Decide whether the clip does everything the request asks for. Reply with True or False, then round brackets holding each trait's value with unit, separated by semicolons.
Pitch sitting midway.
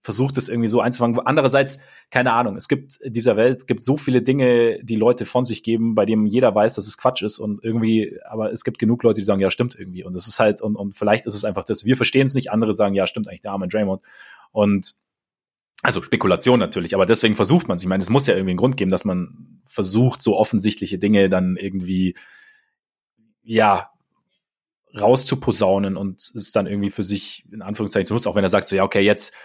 False (110 Hz)